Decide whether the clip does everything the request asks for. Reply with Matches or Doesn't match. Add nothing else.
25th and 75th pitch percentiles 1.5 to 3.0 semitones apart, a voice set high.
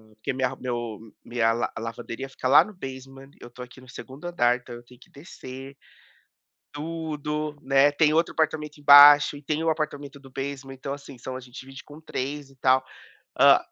Doesn't match